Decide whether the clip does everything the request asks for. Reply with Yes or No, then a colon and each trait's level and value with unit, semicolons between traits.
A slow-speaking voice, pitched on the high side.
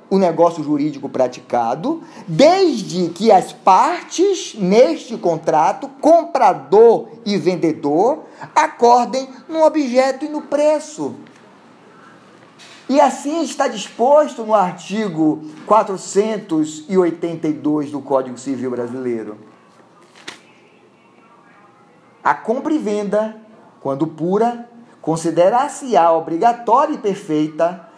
Yes: slow, 85 wpm; high, 210 Hz